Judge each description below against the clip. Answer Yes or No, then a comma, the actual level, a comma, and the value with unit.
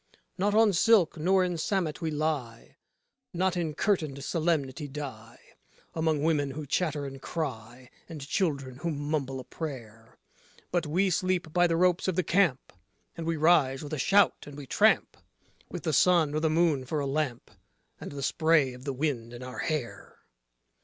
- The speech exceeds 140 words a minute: Yes, average, 175 wpm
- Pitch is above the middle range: No, medium, 155 Hz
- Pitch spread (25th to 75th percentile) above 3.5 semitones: Yes, average, 4.1 semitones